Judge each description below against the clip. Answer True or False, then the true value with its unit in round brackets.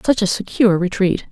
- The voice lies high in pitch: True (195 Hz)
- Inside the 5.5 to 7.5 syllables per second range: True (5.9 syllables/s)